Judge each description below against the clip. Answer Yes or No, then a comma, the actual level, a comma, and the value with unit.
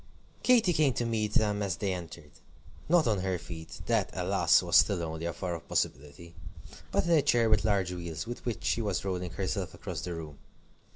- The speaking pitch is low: Yes, very low, 95 Hz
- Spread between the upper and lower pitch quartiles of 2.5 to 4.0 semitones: No, average, 4.7 semitones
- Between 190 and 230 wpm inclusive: Yes, fast, 205 wpm